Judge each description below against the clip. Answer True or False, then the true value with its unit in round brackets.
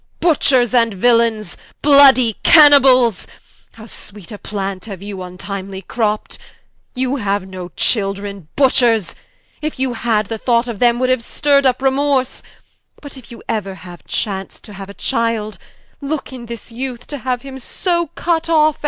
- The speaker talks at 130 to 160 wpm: True (155 wpm)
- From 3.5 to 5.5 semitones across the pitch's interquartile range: True (4.7 semitones)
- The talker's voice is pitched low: False (235 Hz)